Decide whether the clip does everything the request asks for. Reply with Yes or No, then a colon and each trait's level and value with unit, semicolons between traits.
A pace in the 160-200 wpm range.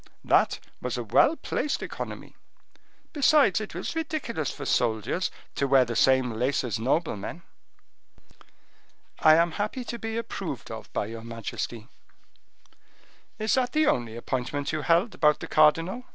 No: average, 145 wpm